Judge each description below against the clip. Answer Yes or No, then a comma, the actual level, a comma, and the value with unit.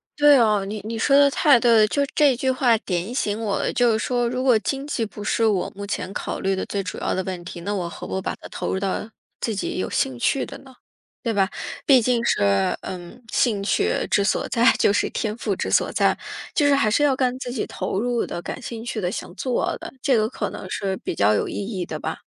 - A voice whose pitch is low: No, high, 220 Hz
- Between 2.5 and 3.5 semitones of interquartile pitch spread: No, average, 4.4 semitones